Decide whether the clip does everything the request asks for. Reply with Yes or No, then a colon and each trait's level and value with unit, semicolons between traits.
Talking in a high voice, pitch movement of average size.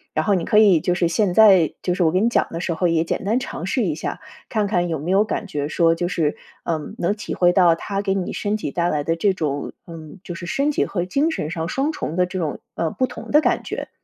No: medium, 180 Hz; average, 3.7 semitones